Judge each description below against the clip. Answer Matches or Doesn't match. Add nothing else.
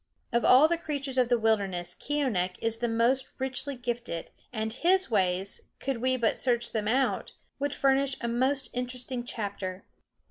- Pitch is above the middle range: Matches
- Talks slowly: Doesn't match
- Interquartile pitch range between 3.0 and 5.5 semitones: Matches